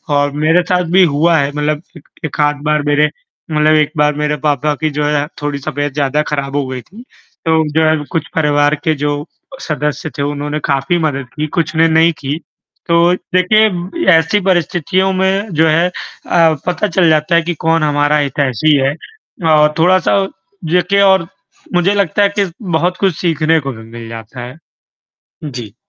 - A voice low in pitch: No, medium, 155 Hz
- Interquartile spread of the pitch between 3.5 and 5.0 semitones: No, average, 3.0 semitones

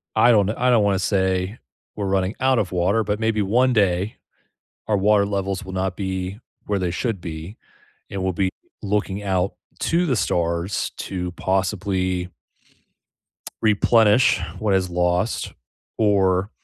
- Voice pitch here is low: Yes, low, 100 Hz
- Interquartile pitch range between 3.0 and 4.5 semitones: No, narrow, 2.4 semitones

